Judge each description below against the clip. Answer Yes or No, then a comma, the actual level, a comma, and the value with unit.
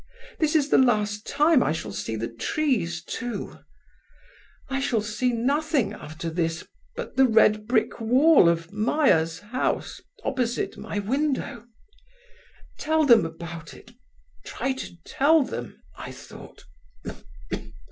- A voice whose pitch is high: Yes, high, 230 Hz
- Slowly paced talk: Yes, slow, 125 wpm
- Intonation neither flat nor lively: No, wide, 7.9 semitones